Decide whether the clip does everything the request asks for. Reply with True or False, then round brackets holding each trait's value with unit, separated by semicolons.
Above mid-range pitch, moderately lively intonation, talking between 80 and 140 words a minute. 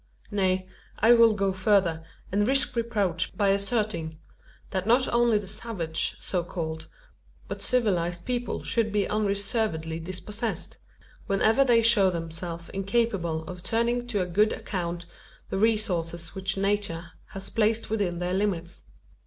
True (195 Hz; 4.2 semitones; 135 wpm)